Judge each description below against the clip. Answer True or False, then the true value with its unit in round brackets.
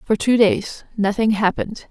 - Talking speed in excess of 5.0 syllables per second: False (4.7 syllables/s)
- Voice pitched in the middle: False (210 Hz)